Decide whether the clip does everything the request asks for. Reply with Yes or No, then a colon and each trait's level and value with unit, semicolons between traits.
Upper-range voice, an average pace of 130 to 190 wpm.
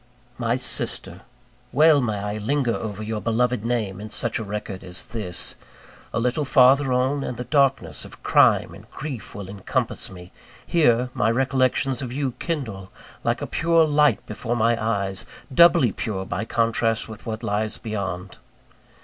No: low, 115 Hz; average, 160 wpm